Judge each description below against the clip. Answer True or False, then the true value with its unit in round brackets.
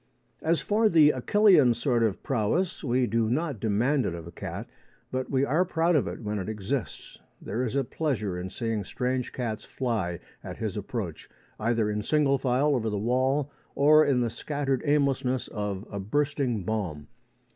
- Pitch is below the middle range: True (125 Hz)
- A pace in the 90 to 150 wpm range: False (180 wpm)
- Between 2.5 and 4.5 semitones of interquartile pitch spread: False (5.0 semitones)